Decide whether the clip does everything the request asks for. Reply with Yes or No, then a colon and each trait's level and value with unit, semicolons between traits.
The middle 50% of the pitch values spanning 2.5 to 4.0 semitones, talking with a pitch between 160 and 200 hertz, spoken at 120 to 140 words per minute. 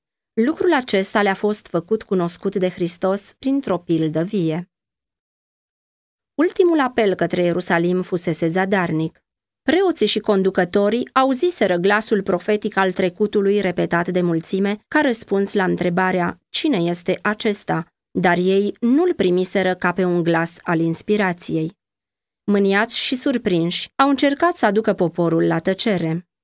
Yes: average, 3.6 semitones; high, 190 Hz; average, 125 wpm